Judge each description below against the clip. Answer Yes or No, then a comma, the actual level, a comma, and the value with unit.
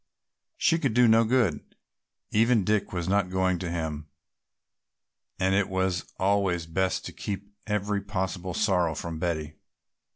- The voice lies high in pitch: No, very low, 95 Hz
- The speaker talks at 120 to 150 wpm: Yes, average, 140 wpm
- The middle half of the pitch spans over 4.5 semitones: No, average, 3.2 semitones